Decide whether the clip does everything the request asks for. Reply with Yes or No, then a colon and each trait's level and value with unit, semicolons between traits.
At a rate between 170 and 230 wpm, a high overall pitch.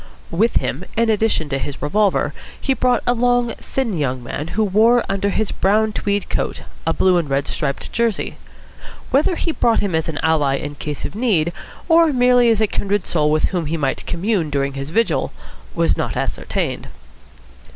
Yes: average, 185 wpm; high, 200 Hz